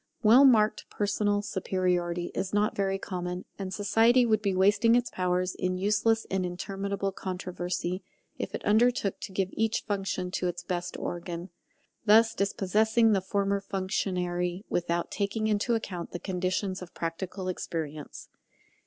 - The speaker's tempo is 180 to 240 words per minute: No, average, 145 wpm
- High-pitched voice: Yes, high, 195 Hz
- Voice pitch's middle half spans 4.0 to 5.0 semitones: No, narrow, 2.6 semitones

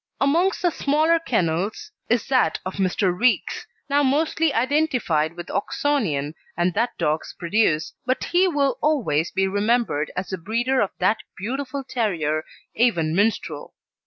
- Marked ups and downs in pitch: Yes, wide, 8.0 semitones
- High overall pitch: Yes, high, 225 Hz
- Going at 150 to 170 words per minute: No, average, 140 wpm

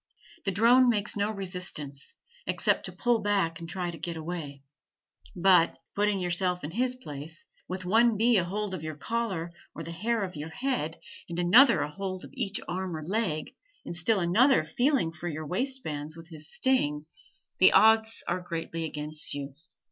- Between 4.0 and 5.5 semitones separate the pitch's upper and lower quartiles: Yes, average, 5.2 semitones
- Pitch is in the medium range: Yes, medium, 180 Hz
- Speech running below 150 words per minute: No, average, 180 wpm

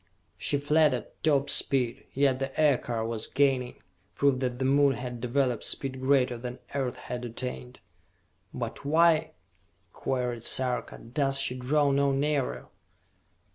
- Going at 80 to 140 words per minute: Yes, slow, 135 wpm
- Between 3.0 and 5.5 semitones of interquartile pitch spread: No, narrow, 2.4 semitones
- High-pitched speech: No, low, 135 Hz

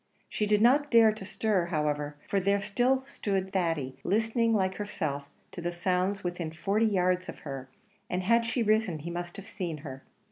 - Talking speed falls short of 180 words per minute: No, average, 185 wpm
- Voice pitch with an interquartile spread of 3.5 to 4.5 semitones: Yes, average, 4.1 semitones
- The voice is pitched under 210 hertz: Yes, high, 190 Hz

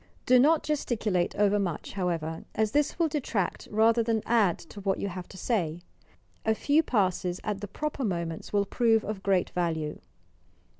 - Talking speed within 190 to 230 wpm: No, average, 165 wpm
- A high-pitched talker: Yes, high, 205 Hz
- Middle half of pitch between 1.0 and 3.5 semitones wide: No, average, 4.4 semitones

